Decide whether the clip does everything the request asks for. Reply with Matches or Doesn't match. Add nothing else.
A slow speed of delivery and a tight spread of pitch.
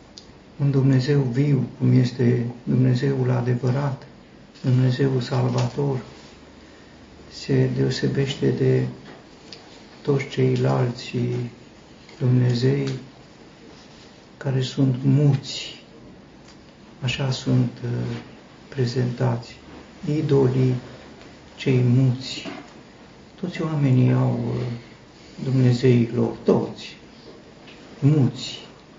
Matches